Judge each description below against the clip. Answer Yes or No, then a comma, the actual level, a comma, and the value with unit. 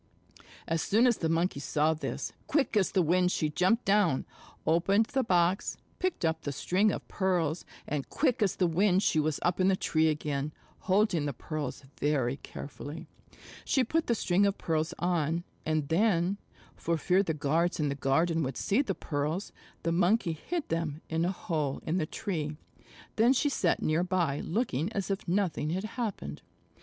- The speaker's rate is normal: Yes, average, 180 wpm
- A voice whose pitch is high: No, medium, 170 Hz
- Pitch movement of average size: Yes, average, 4.2 semitones